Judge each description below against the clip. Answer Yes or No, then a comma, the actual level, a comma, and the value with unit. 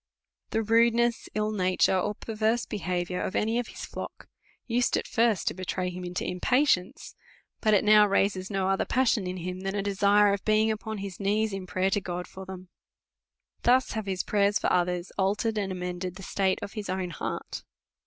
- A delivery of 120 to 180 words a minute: No, fast, 205 wpm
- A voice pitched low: No, high, 195 Hz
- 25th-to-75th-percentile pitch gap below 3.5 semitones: Yes, average, 2.8 semitones